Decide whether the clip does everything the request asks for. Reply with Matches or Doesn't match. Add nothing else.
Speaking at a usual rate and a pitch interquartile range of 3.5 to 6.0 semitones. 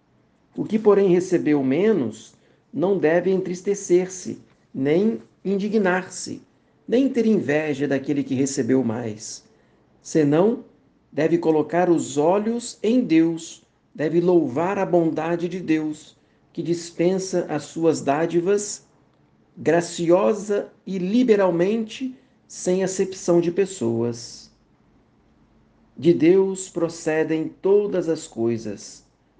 Doesn't match